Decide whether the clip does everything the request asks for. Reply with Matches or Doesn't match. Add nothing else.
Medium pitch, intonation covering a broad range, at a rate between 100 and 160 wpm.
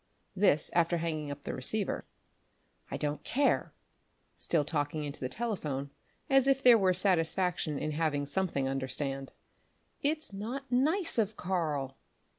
Matches